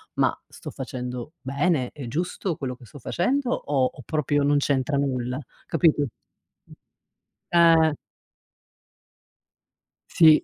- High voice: No, medium, 145 Hz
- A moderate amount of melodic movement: Yes, average, 4.0 semitones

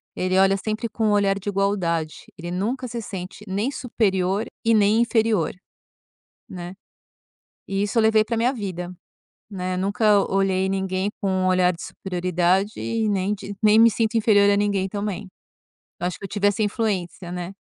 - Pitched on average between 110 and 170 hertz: No, high, 200 Hz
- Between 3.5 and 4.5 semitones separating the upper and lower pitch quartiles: No, narrow, 2.6 semitones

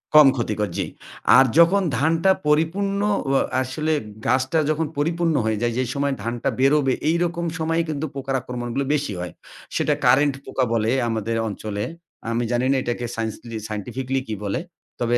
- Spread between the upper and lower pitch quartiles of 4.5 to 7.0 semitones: Yes, average, 5.2 semitones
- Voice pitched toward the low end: Yes, low, 130 Hz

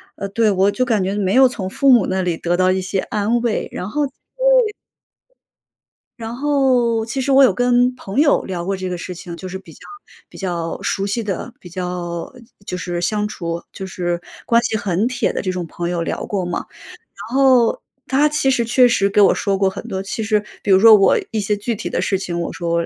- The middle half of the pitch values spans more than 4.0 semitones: Yes, average, 4.5 semitones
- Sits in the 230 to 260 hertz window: No, high, 200 Hz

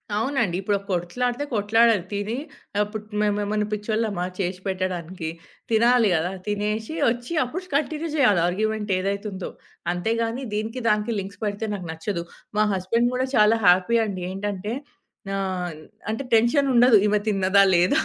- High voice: Yes, high, 210 Hz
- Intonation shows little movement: No, average, 3.3 semitones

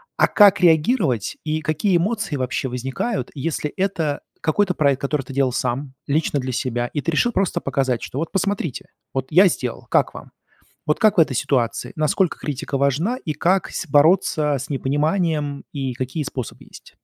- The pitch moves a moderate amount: Yes, average, 4.5 semitones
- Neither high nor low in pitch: Yes, medium, 150 Hz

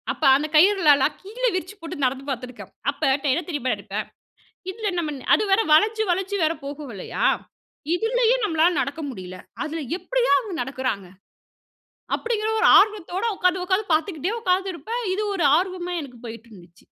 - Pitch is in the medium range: No, very high, 345 Hz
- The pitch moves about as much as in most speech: No, wide, 6.5 semitones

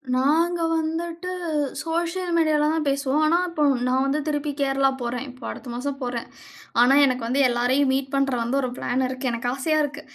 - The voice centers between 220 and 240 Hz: No, very high, 275 Hz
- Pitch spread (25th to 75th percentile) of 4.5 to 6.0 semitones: No, average, 3.4 semitones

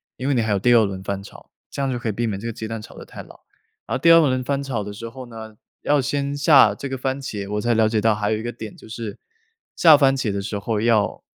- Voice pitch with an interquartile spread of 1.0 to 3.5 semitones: No, average, 3.9 semitones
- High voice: No, low, 115 Hz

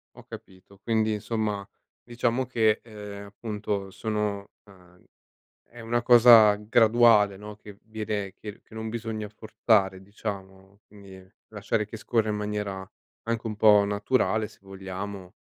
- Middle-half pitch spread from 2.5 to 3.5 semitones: No, narrow, 1.9 semitones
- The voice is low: Yes, low, 105 Hz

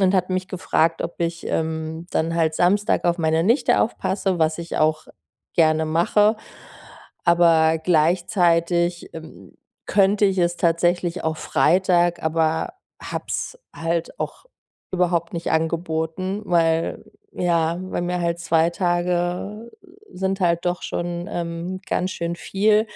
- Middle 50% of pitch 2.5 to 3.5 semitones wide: No, narrow, 2.0 semitones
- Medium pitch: Yes, medium, 170 Hz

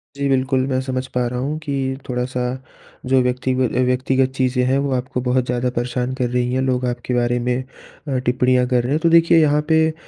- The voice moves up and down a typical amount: No, narrow, 1.2 semitones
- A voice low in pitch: Yes, low, 130 Hz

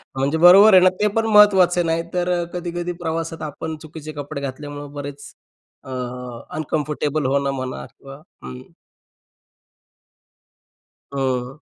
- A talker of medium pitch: Yes, medium, 155 Hz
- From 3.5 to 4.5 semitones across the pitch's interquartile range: Yes, average, 3.9 semitones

